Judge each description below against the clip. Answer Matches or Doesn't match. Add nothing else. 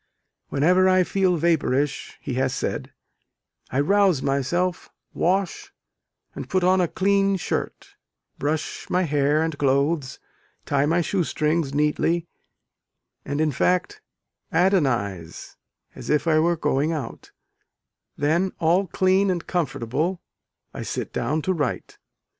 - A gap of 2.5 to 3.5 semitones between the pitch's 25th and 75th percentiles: Doesn't match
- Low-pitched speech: Doesn't match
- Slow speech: Matches